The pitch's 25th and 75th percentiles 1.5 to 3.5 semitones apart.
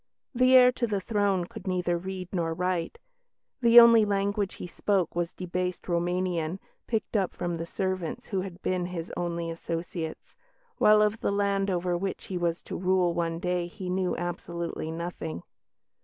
Yes: narrow, 2.4 semitones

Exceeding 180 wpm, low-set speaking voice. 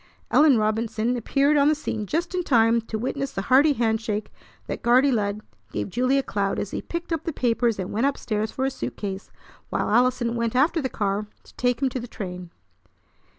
No: fast, 205 wpm; high, 235 Hz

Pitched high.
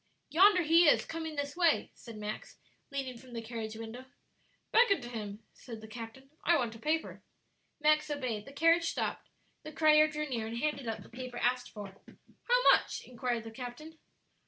Yes: very high, 260 Hz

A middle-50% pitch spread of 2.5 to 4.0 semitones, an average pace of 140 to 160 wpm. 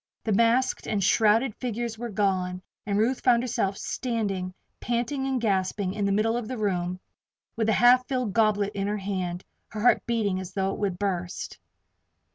No: average, 3.5 semitones; average, 180 wpm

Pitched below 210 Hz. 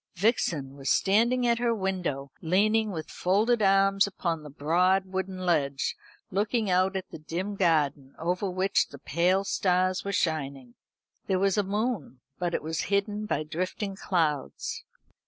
Yes: medium, 185 Hz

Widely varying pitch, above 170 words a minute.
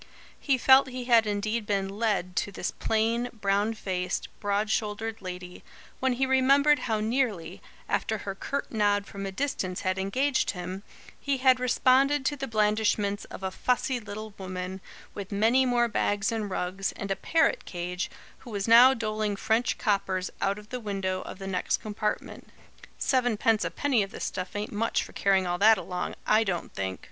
No: average, 3.8 semitones; average, 180 wpm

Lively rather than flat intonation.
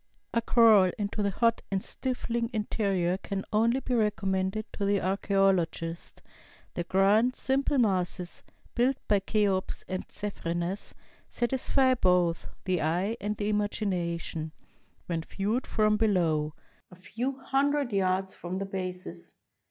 No: average, 3.7 semitones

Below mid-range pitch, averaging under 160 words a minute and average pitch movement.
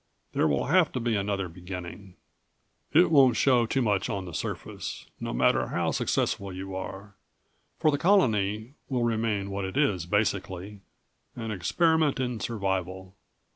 Yes: low, 105 Hz; average, 150 wpm; average, 4.7 semitones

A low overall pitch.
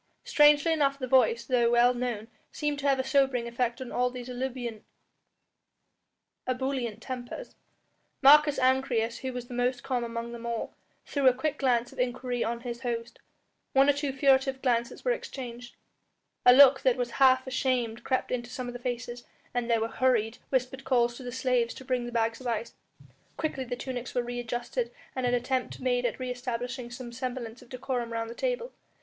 No: very high, 250 Hz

